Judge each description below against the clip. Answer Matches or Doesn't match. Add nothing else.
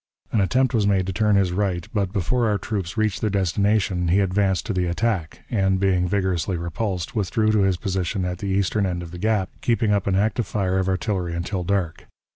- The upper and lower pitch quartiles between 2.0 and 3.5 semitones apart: Matches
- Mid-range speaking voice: Doesn't match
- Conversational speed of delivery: Doesn't match